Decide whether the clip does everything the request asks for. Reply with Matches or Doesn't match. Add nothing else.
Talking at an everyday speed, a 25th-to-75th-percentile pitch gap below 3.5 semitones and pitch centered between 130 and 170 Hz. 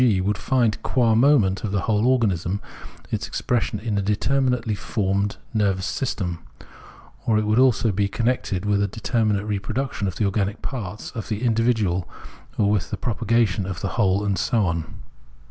Doesn't match